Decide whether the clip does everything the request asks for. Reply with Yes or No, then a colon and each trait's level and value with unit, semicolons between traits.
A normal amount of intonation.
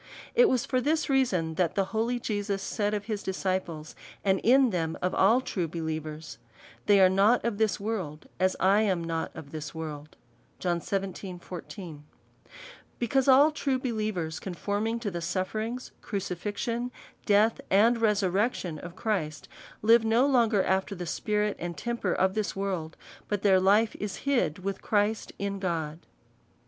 Yes: average, 4.2 semitones